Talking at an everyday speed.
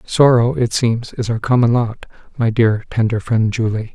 Yes: average, 180 wpm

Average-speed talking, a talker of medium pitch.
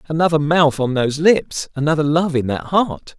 Yes: average, 190 wpm; medium, 150 Hz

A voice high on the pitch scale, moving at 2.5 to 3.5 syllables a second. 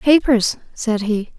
Yes: high, 235 Hz; 3.4 syllables/s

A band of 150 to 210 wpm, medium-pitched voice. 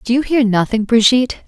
No: fast, 205 wpm; high, 235 Hz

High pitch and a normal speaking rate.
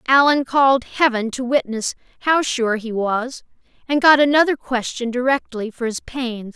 Yes: very high, 250 Hz; average, 155 wpm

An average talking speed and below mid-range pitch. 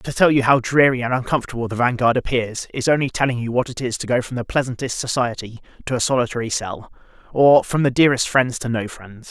No: fast, 225 wpm; low, 125 Hz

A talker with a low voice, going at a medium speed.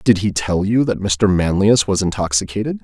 Yes: low, 100 Hz; average, 190 wpm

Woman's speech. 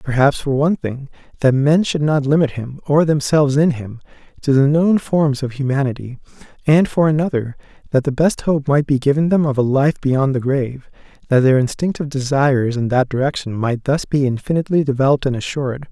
No: male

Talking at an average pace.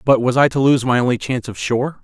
No: fast, 295 wpm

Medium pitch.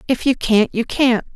No: high, 240 Hz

